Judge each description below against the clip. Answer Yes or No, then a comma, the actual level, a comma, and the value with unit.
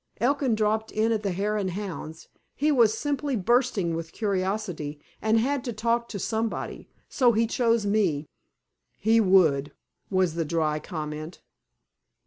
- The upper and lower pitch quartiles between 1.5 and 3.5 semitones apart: No, average, 5.2 semitones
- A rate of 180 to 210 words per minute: No, average, 145 wpm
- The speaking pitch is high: Yes, high, 210 Hz